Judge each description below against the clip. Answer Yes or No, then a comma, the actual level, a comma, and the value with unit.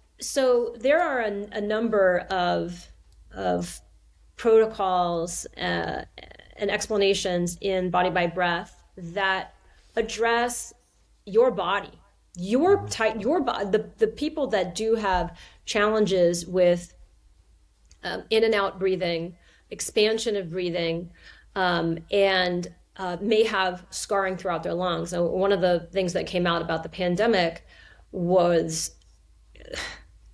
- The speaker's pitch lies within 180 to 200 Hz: Yes, medium, 185 Hz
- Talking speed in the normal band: No, slow, 120 wpm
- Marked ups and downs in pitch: No, average, 3.9 semitones